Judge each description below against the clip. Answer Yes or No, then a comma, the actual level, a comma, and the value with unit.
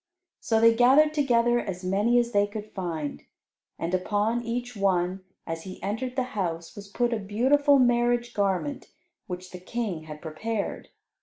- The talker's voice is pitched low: No, high, 215 Hz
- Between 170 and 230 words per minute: No, average, 160 wpm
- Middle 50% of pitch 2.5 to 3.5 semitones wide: No, average, 4.6 semitones